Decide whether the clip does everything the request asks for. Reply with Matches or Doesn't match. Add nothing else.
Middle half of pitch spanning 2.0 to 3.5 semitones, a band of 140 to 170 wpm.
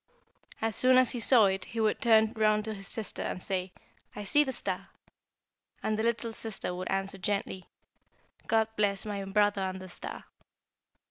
Doesn't match